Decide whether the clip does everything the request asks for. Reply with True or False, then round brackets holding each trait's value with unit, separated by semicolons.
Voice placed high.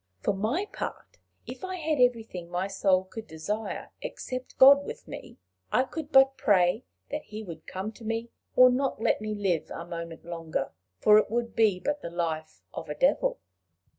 True (215 Hz)